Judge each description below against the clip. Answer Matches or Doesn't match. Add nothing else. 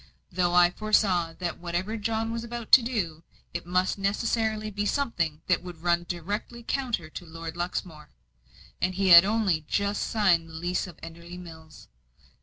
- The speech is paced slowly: Doesn't match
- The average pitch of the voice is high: Doesn't match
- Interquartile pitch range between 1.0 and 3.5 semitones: Doesn't match